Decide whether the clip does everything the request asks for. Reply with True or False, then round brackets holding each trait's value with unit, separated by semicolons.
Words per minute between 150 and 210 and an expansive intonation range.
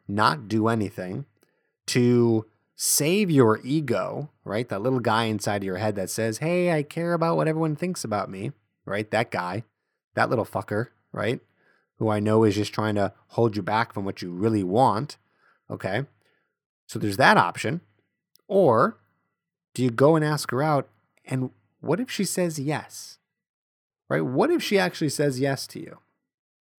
True (170 wpm; 6.2 semitones)